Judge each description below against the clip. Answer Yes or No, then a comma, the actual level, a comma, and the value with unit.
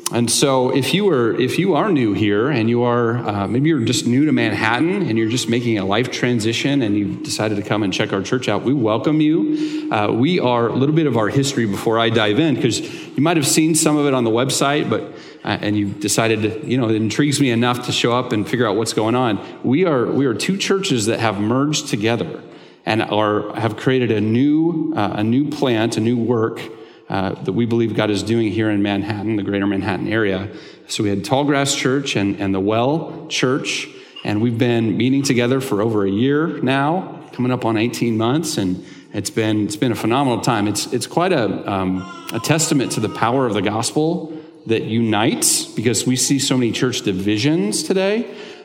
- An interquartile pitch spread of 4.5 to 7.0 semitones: Yes, average, 4.8 semitones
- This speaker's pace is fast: Yes, fast, 220 wpm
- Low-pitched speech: Yes, low, 120 Hz